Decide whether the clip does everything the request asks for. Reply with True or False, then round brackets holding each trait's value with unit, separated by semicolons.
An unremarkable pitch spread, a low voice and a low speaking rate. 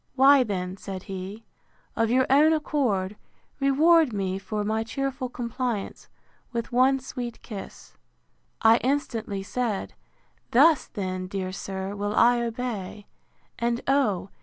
False (4.8 semitones; 230 Hz; 120 wpm)